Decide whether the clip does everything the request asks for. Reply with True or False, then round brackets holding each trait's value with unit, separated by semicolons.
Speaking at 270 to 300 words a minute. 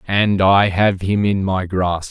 False (200 wpm)